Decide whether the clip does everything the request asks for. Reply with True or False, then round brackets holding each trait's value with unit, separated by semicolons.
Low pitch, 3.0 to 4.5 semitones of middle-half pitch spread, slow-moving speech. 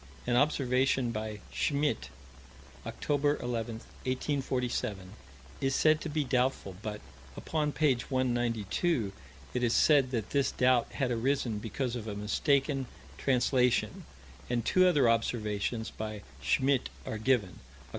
True (125 Hz; 3.7 semitones; 125 wpm)